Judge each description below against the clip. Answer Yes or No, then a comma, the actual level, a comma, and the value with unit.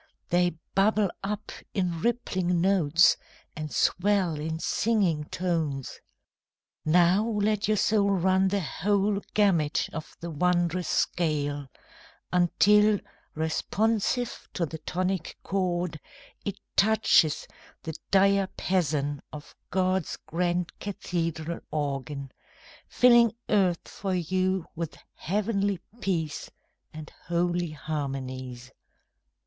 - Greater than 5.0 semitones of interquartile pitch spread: No, average, 4.0 semitones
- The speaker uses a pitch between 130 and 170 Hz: No, medium, 180 Hz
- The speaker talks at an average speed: No, slow, 100 wpm